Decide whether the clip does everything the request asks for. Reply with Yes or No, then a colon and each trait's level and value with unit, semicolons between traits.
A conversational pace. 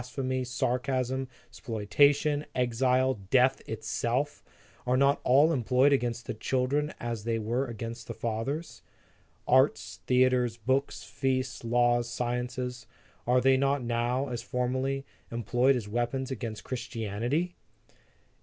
No: slow, 120 wpm